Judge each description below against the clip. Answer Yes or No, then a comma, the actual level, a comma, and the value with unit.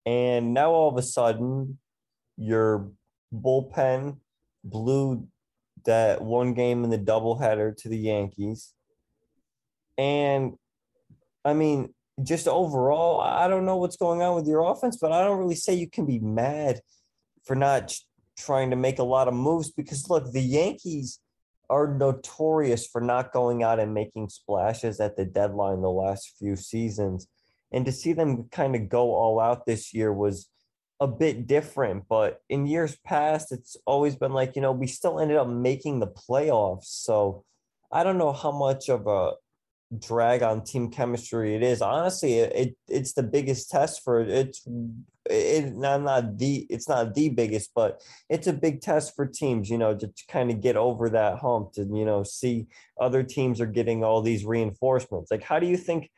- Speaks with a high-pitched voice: No, low, 125 Hz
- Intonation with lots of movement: No, average, 4.0 semitones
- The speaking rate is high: No, average, 180 wpm